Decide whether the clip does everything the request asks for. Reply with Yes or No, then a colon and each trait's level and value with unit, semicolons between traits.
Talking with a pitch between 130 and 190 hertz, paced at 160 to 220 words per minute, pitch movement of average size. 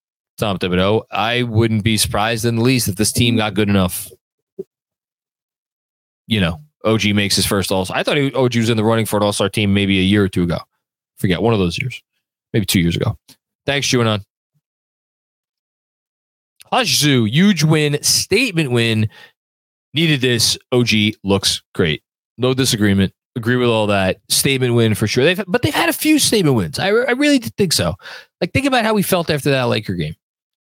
No: low, 115 Hz; average, 190 wpm; average, 4.9 semitones